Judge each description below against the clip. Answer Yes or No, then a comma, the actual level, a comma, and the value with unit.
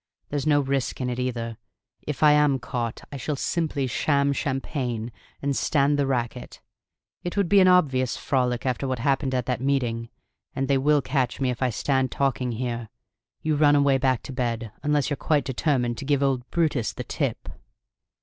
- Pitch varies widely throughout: No, narrow, 2.6 semitones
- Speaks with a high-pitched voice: No, low, 135 Hz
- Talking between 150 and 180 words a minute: No, average, 190 wpm